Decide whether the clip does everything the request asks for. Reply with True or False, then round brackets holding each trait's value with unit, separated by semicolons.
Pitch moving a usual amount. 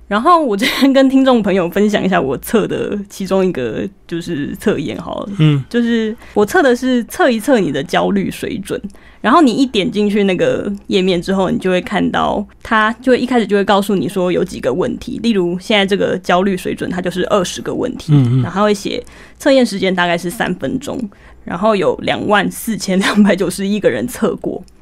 True (4.7 semitones)